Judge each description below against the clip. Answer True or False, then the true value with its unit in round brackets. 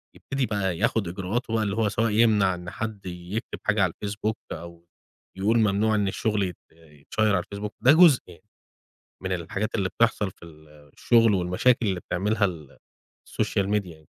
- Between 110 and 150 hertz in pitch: False (100 Hz)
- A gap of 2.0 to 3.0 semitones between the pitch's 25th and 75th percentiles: False (3.6 semitones)